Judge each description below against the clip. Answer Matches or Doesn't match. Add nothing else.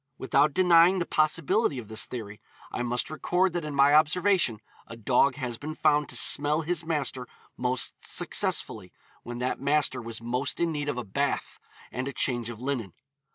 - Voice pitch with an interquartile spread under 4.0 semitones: Doesn't match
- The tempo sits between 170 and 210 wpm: Matches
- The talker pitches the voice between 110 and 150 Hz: Matches